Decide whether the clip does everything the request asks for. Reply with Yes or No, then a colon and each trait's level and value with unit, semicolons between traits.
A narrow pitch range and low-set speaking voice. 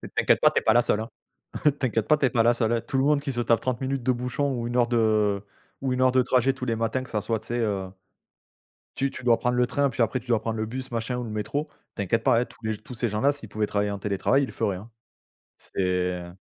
No: average, 3.0 semitones; low, 115 Hz